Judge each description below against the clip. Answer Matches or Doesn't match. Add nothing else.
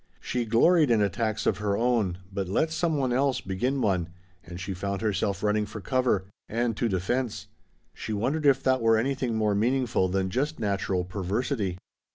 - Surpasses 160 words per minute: Matches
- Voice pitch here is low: Matches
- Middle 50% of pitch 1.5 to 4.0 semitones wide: Doesn't match